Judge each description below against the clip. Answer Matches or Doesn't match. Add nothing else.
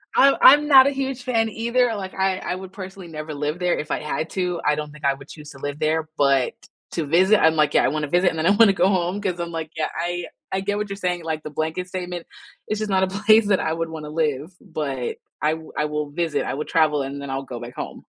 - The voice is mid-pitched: Matches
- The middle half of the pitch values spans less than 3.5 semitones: Doesn't match